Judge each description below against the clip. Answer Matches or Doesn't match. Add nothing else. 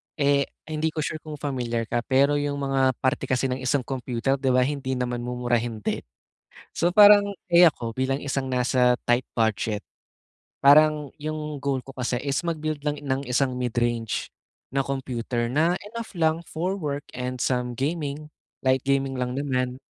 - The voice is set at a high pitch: Doesn't match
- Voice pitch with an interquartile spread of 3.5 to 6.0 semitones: Doesn't match